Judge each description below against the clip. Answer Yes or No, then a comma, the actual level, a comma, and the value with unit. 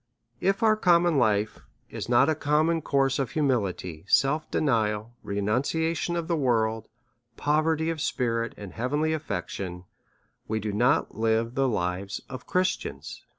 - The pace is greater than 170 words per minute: No, average, 145 wpm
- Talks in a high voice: No, low, 130 Hz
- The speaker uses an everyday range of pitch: No, wide, 6.4 semitones